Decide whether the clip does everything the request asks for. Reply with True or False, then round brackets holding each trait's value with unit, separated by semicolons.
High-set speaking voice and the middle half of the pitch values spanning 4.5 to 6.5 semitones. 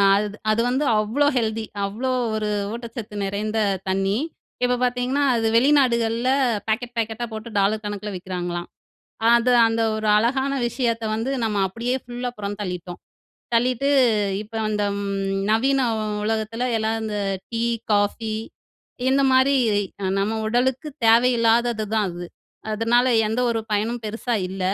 False (225 Hz; 2.7 semitones)